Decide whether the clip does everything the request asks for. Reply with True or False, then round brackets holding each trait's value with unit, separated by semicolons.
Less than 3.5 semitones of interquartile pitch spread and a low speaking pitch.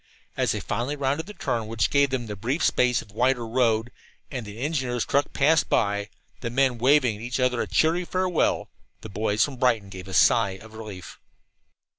False (4.0 semitones; 120 Hz)